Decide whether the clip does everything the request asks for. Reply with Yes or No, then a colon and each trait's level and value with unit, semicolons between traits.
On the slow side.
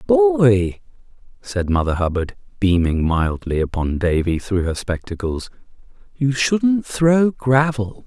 Yes: slow, 110 wpm